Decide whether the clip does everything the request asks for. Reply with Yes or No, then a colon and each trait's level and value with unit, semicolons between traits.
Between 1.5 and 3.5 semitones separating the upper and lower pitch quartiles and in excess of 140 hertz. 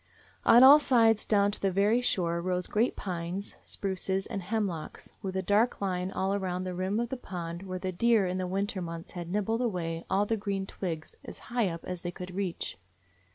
Yes: narrow, 2.5 semitones; high, 190 Hz